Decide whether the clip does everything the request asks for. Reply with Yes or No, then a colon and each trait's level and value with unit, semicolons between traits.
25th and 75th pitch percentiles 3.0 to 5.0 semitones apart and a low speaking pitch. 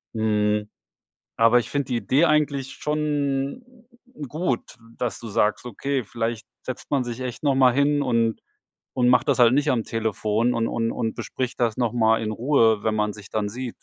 Yes: average, 3.4 semitones; low, 120 Hz